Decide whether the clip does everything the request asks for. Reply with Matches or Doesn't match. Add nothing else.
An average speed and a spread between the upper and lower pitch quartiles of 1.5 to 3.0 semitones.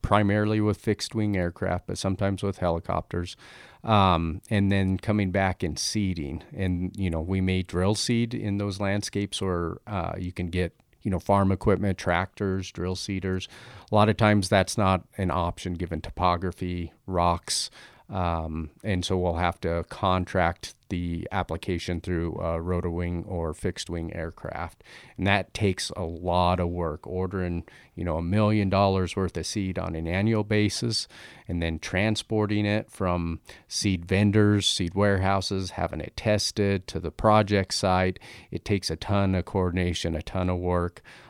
Matches